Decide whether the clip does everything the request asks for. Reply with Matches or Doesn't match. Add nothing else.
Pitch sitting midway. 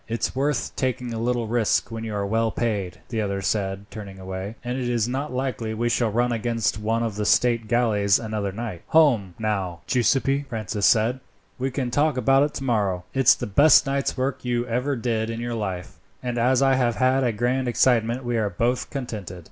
Doesn't match